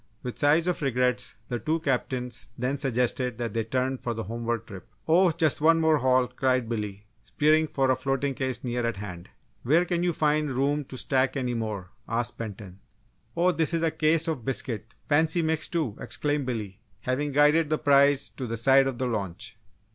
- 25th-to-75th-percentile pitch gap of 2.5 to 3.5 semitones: No, average, 4.4 semitones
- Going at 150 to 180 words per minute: No, average, 195 wpm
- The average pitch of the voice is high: No, low, 130 Hz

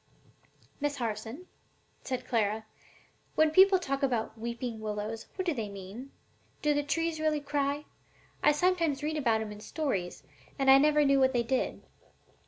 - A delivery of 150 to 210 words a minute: Yes, average, 165 wpm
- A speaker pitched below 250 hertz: No, very high, 270 Hz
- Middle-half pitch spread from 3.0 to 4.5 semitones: No, average, 5.1 semitones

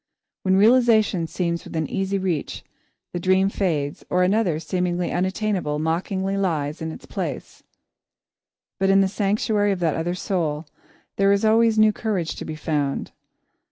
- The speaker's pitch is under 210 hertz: Yes, medium, 185 Hz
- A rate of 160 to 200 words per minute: No, average, 145 wpm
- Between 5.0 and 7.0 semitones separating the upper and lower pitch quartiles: No, average, 3.4 semitones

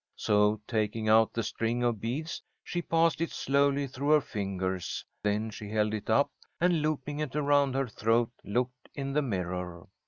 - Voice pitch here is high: No, low, 120 Hz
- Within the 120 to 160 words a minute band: No, average, 175 wpm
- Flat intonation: No, average, 5.1 semitones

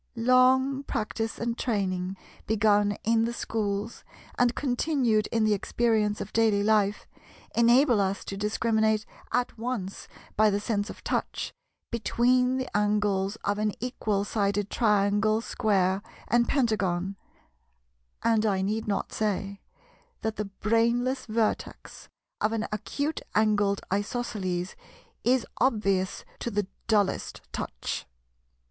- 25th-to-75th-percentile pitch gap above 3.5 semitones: No, narrow, 2.6 semitones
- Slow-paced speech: Yes, slow, 120 wpm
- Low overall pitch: No, high, 215 Hz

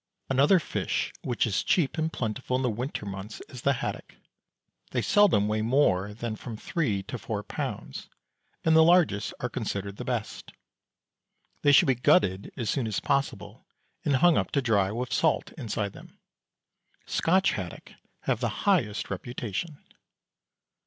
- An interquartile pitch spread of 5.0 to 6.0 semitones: Yes, wide, 5.4 semitones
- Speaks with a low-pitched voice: Yes, low, 120 Hz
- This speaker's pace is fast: No, average, 155 wpm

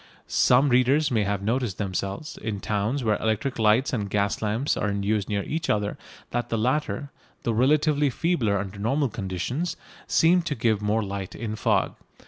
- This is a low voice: Yes, low, 110 Hz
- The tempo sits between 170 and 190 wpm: Yes, average, 175 wpm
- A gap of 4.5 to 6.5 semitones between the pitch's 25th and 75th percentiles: Yes, average, 5.1 semitones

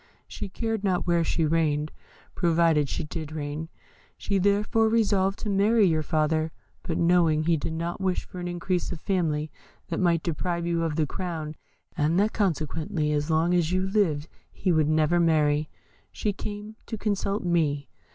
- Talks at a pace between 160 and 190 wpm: Yes, average, 170 wpm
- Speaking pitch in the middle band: Yes, medium, 170 Hz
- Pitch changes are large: No, average, 3.6 semitones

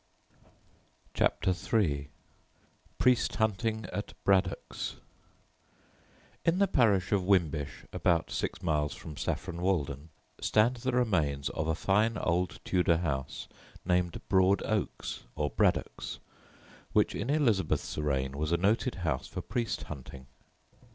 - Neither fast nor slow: No, slow, 120 wpm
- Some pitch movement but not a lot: No, wide, 6.2 semitones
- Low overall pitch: Yes, very low, 90 Hz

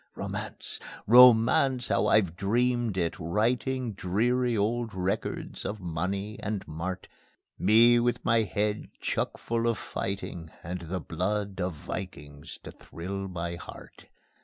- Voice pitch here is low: Yes, low, 100 Hz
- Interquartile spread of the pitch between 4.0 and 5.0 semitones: Yes, average, 4.4 semitones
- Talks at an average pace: No, slow, 125 wpm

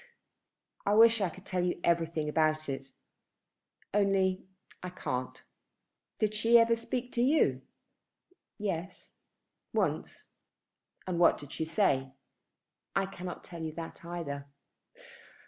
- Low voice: No, medium, 180 Hz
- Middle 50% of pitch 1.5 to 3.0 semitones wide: No, average, 4.5 semitones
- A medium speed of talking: No, slow, 120 wpm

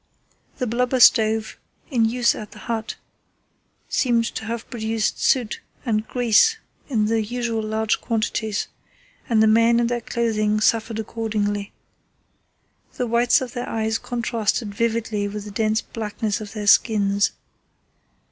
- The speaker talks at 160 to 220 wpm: No, average, 140 wpm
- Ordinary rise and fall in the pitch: No, narrow, 1.7 semitones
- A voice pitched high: Yes, high, 225 Hz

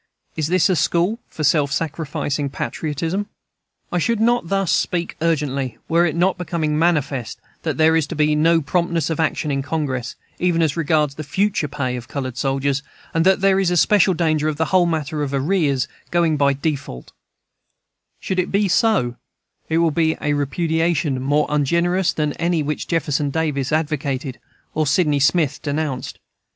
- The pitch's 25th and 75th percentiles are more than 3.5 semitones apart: No, average, 3.2 semitones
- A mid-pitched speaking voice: Yes, medium, 155 Hz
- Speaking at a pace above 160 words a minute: Yes, average, 170 wpm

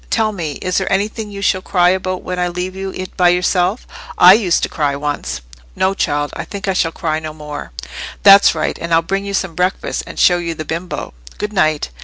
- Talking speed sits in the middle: No, fast, 220 wpm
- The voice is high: No, medium, 180 Hz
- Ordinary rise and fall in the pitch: Yes, average, 3.0 semitones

